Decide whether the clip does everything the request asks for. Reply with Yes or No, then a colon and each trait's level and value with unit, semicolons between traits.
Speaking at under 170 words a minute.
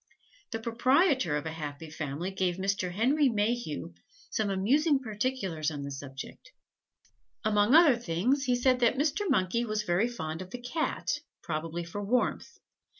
Yes: average, 150 wpm